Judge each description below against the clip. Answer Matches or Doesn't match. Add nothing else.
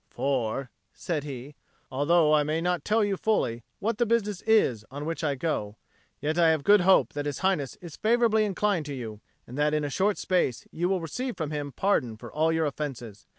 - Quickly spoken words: Matches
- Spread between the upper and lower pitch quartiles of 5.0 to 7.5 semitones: Matches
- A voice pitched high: Doesn't match